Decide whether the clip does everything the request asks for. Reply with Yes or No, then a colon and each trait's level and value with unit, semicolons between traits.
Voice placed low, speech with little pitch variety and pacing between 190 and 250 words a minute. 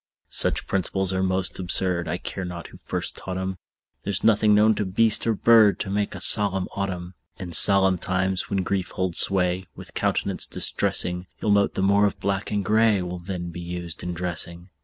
Yes: very low, 95 Hz; narrow, 2.1 semitones; average, 195 wpm